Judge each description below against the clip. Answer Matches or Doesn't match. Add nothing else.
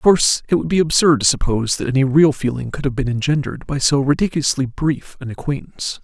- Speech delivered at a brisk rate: Matches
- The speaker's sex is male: Matches